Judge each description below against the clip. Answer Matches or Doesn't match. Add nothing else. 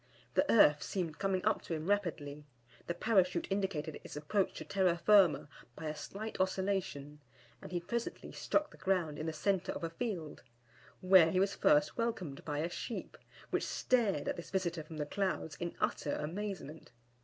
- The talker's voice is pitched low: Doesn't match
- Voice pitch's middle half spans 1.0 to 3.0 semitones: Doesn't match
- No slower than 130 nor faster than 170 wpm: Doesn't match